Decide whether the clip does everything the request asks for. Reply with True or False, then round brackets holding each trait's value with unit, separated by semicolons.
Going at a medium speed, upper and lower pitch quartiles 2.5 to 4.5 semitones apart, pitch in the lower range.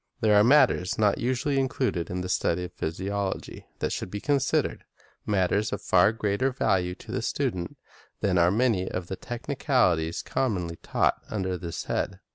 False (170 wpm; 5.2 semitones; 100 Hz)